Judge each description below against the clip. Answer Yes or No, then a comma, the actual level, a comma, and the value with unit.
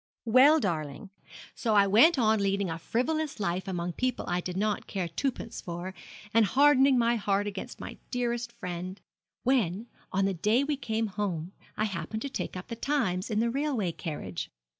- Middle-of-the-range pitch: No, high, 210 Hz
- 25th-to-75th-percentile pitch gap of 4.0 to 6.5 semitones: Yes, average, 5.0 semitones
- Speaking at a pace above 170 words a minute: Yes, average, 180 wpm